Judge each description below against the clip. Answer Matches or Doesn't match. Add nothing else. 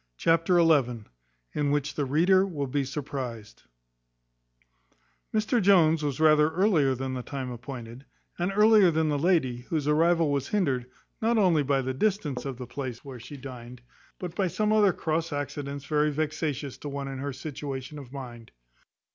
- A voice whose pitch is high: Doesn't match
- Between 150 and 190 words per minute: Matches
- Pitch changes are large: Doesn't match